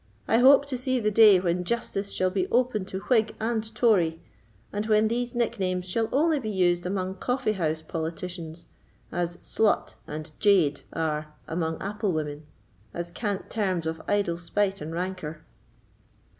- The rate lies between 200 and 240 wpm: No, average, 155 wpm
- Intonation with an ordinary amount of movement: Yes, average, 4.5 semitones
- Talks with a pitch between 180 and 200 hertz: Yes, high, 190 Hz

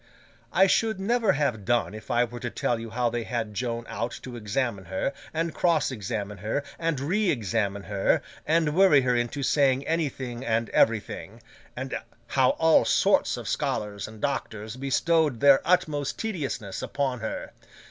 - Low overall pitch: Yes, low, 125 Hz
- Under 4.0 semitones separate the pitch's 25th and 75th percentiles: No, average, 5.2 semitones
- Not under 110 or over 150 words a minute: No, average, 165 wpm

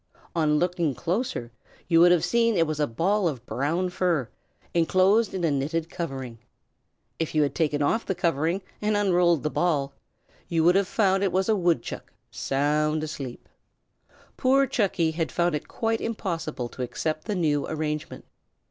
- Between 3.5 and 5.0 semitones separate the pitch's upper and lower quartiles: Yes, average, 3.8 semitones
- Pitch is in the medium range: Yes, medium, 165 Hz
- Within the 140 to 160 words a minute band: No, average, 175 wpm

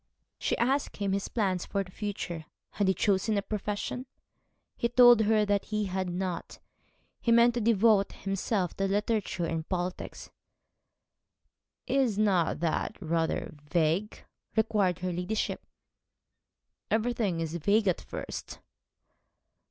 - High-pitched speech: Yes, high, 200 Hz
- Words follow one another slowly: Yes, slow, 130 wpm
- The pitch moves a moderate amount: Yes, average, 3.4 semitones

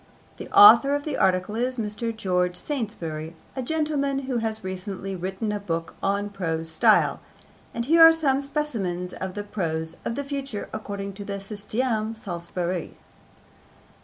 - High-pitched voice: Yes, high, 205 Hz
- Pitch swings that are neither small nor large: No, wide, 6.2 semitones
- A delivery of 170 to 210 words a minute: No, average, 160 wpm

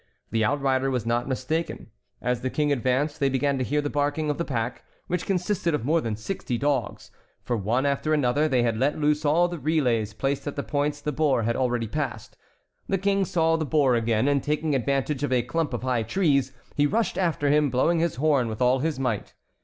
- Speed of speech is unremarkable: No, fast, 215 wpm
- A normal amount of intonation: Yes, average, 3.6 semitones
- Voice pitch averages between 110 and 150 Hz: Yes, medium, 140 Hz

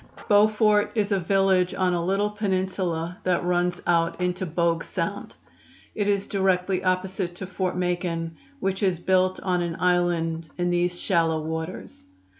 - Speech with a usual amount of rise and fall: No, narrow, 1.8 semitones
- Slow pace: No, average, 150 wpm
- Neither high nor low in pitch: Yes, medium, 180 Hz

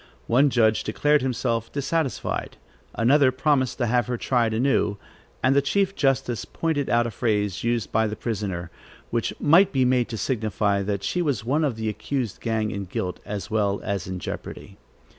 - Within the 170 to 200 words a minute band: Yes, average, 180 wpm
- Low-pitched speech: Yes, low, 120 Hz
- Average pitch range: Yes, average, 4.2 semitones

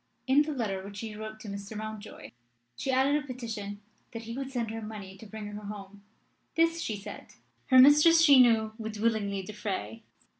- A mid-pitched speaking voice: No, high, 220 Hz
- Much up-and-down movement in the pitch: No, average, 4.0 semitones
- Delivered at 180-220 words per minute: Yes, average, 190 wpm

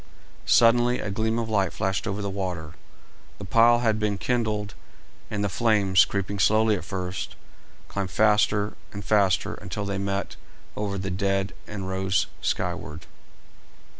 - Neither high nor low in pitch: No, low, 100 Hz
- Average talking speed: Yes, average, 145 wpm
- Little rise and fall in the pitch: Yes, narrow, 2.2 semitones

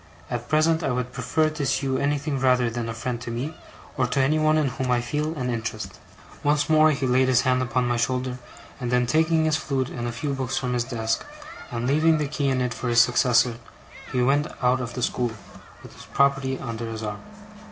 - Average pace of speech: No, fast, 225 wpm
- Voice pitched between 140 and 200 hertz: No, low, 130 Hz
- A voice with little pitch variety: No, average, 3.0 semitones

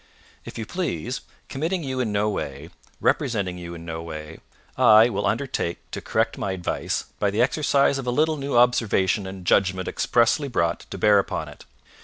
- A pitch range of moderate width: No, wide, 6.3 semitones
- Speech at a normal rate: Yes, average, 180 wpm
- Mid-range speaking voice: No, low, 105 Hz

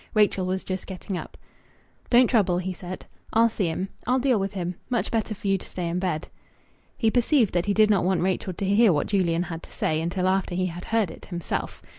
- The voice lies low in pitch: No, high, 190 Hz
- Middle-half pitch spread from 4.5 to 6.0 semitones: No, average, 3.3 semitones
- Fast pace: Yes, fast, 230 wpm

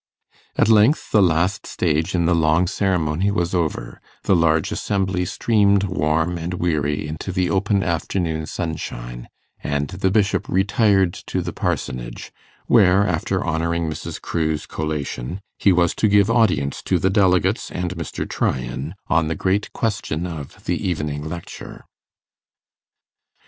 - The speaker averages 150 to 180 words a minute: No, average, 140 wpm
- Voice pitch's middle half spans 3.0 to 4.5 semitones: Yes, average, 3.6 semitones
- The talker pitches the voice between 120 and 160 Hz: No, very low, 85 Hz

